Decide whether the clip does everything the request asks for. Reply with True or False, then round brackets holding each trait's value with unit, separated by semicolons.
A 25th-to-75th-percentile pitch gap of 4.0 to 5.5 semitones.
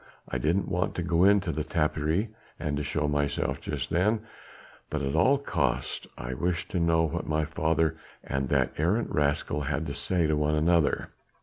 False (3.0 semitones)